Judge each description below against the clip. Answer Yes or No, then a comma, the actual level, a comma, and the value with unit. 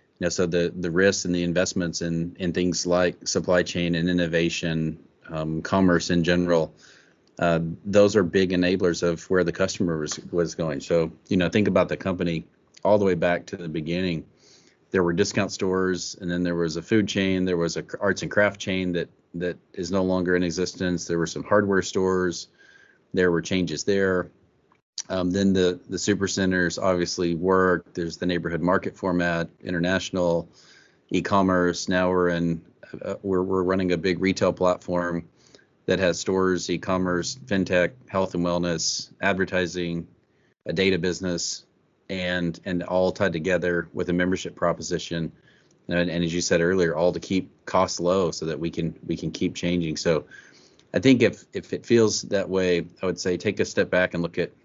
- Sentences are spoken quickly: No, average, 180 wpm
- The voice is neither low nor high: No, very low, 90 Hz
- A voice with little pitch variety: Yes, narrow, 1.5 semitones